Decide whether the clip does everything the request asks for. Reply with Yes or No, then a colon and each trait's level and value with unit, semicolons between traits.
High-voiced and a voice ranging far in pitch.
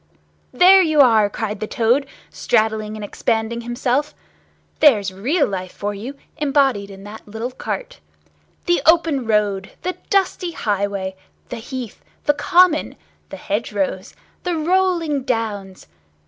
Yes: high, 235 Hz; wide, 6.6 semitones